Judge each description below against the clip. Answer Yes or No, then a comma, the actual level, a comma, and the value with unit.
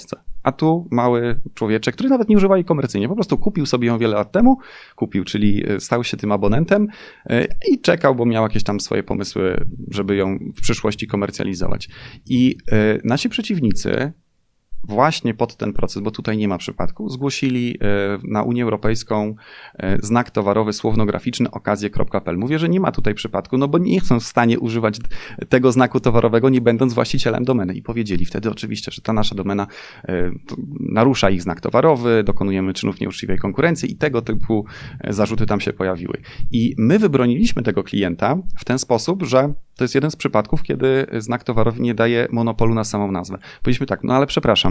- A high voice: No, low, 115 Hz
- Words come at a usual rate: No, fast, 170 wpm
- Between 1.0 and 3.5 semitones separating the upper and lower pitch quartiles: No, average, 4.1 semitones